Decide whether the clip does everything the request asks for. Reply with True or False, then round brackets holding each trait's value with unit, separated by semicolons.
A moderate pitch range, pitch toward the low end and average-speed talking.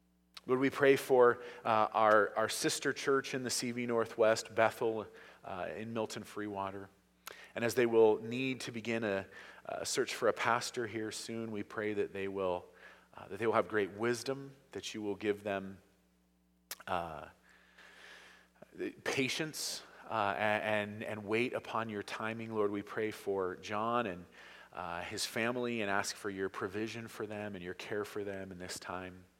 True (3.1 semitones; 110 Hz; 170 wpm)